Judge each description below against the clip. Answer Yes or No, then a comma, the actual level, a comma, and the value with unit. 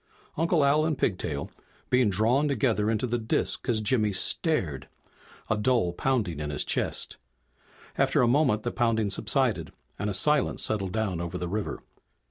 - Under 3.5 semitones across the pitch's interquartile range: No, average, 5.2 semitones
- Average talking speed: Yes, average, 160 wpm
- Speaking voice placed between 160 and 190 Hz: No, low, 110 Hz